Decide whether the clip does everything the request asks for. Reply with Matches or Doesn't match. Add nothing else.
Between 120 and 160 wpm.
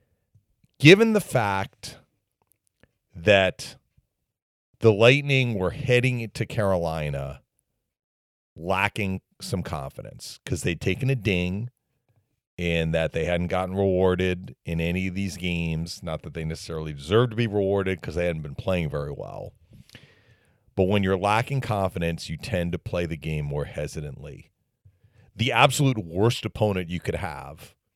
Matches